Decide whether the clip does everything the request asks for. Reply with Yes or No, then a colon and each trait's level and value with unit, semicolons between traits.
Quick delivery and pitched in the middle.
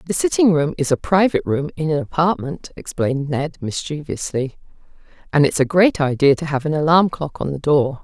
No: average, 195 wpm; medium, 155 Hz